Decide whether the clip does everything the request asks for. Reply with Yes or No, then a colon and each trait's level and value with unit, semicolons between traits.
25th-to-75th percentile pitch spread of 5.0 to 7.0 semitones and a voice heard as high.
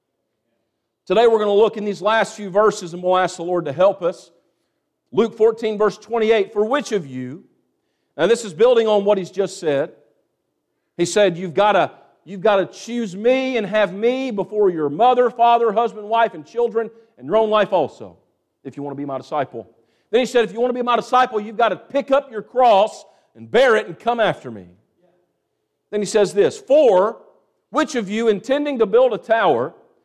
No: average, 4.0 semitones; high, 215 Hz